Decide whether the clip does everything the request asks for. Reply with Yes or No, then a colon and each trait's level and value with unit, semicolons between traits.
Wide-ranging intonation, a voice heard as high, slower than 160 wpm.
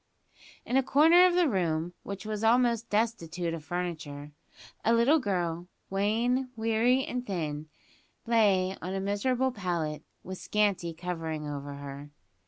Yes: wide, 6.0 semitones; high, 195 Hz; average, 140 wpm